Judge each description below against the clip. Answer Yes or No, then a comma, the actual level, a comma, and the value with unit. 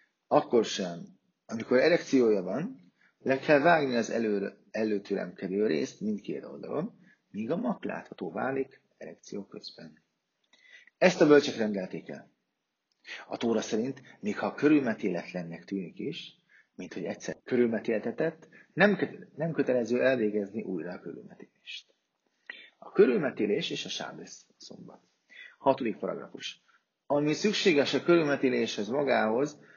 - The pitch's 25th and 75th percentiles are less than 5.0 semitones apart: No, wide, 5.5 semitones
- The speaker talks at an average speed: Yes, average, 115 wpm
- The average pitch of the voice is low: Yes, low, 130 Hz